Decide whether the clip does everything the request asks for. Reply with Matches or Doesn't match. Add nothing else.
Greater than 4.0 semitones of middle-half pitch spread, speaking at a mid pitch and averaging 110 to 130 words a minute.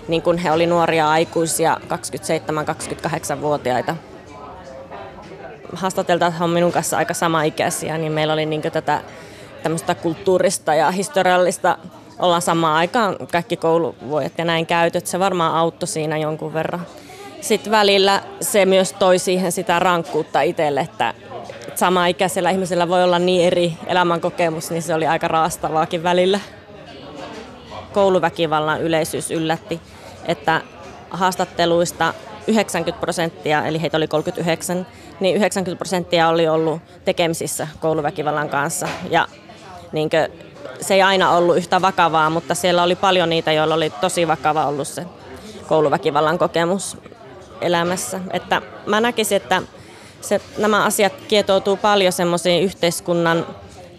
Doesn't match